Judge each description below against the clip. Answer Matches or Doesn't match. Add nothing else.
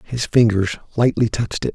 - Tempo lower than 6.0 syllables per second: Matches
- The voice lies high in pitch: Doesn't match